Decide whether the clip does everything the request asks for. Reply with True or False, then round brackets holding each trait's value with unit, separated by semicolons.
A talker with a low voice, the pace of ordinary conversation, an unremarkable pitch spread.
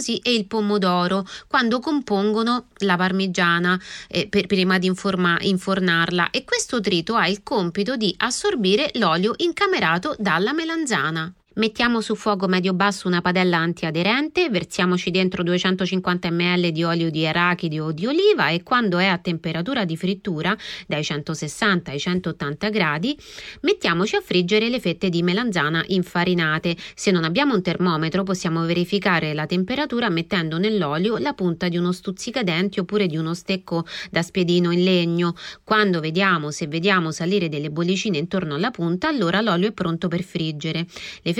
False (185 Hz; 150 wpm; 3.4 semitones)